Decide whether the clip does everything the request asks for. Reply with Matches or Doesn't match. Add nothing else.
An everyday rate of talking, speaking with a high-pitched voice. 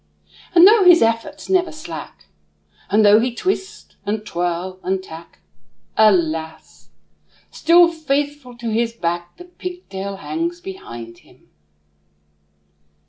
Doesn't match